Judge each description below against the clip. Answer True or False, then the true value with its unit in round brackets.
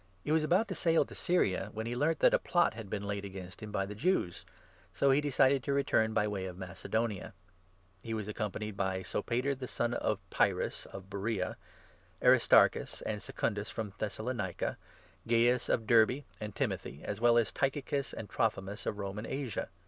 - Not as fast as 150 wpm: False (195 wpm)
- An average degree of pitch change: True (4.4 semitones)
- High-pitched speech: False (110 Hz)